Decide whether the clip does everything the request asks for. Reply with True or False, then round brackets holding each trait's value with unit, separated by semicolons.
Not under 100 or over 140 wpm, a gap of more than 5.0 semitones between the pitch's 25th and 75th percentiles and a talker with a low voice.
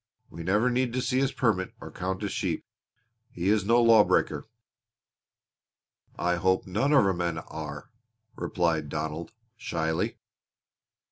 True (135 wpm; 5.5 semitones; 95 Hz)